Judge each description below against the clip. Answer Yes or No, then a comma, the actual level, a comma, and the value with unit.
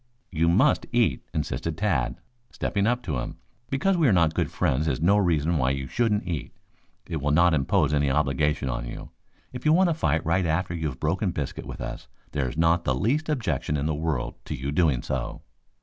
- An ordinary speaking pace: No, fast, 210 wpm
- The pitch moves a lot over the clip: No, average, 4.9 semitones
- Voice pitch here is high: No, very low, 80 Hz